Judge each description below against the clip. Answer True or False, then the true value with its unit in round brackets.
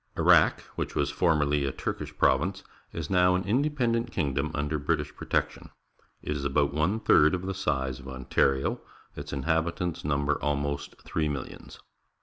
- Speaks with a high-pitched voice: False (75 Hz)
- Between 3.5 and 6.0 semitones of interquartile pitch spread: True (4.1 semitones)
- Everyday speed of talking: True (160 wpm)